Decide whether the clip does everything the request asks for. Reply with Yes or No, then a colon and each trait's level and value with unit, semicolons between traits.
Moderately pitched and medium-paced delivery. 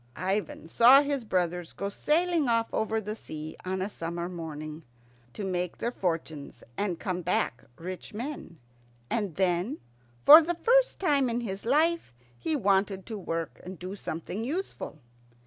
No: high, 195 Hz; average, 155 wpm